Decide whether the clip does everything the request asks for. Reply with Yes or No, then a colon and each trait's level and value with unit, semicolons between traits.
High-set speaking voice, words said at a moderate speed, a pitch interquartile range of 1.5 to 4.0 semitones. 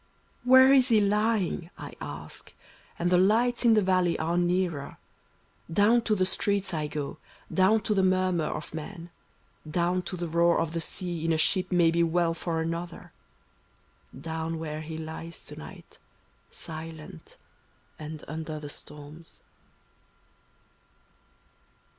No: medium, 170 Hz; average, 145 wpm; average, 2.8 semitones